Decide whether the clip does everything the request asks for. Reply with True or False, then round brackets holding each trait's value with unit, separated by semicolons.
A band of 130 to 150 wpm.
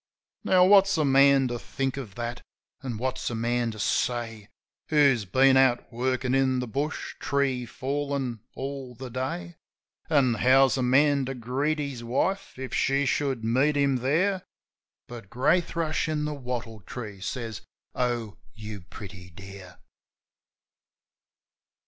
True (145 wpm)